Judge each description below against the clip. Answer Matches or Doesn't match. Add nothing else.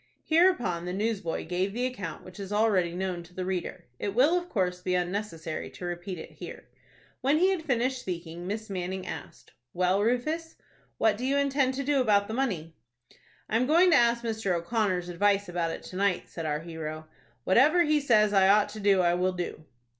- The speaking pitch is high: Matches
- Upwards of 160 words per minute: Matches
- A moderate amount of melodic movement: Doesn't match